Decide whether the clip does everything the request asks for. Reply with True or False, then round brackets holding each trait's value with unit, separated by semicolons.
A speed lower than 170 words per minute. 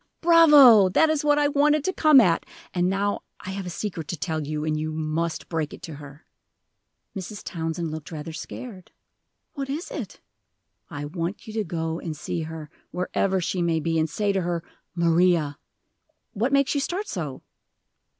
False (180 wpm)